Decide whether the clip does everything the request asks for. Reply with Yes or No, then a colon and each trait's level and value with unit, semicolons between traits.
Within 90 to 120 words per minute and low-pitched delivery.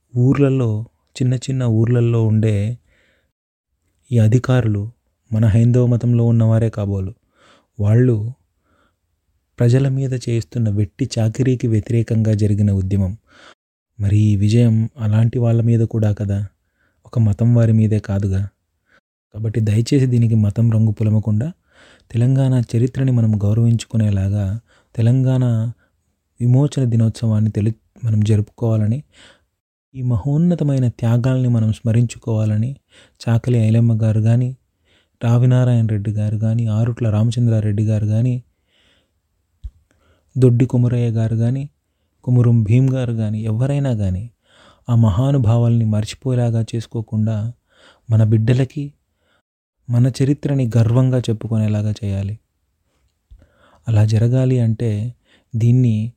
Yes: average, 100 wpm; low, 115 Hz